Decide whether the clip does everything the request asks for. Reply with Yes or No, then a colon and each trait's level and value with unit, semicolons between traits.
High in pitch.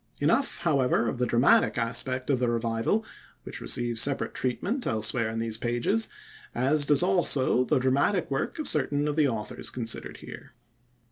No: low, 130 Hz